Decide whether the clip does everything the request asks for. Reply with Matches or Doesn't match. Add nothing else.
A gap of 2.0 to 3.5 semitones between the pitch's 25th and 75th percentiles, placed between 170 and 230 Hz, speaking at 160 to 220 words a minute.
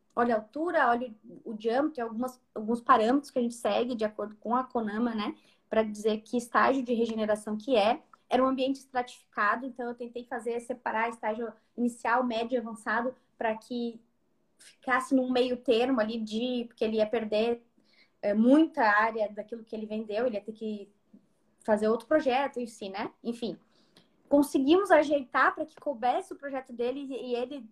Doesn't match